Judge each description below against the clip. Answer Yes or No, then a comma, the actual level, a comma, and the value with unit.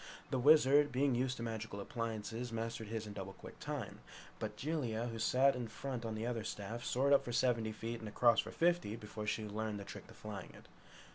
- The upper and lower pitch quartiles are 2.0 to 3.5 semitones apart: Yes, narrow, 2.6 semitones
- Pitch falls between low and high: No, low, 115 Hz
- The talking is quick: Yes, fast, 215 wpm